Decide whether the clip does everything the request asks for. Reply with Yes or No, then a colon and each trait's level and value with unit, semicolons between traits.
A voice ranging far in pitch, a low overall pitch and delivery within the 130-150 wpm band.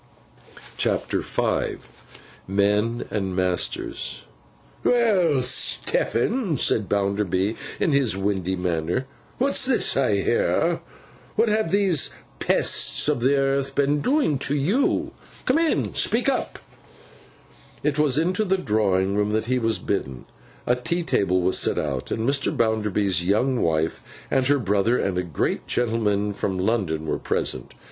Yes: wide, 7.1 semitones; low, 115 Hz; average, 140 wpm